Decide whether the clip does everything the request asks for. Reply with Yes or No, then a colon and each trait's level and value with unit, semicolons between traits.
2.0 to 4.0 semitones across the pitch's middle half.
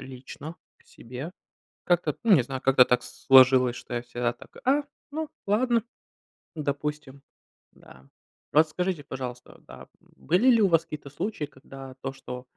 No: average, 5.2 semitones